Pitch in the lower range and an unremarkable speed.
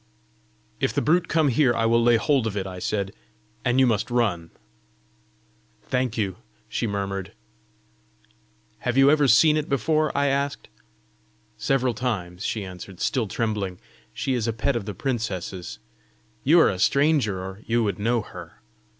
Yes: low, 115 Hz; average, 160 wpm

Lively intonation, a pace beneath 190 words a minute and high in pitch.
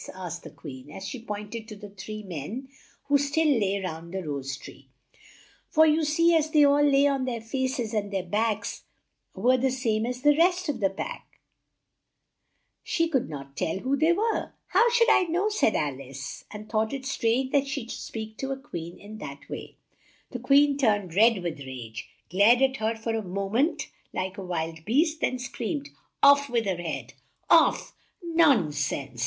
No: wide, 7.0 semitones; average, 195 wpm; high, 225 Hz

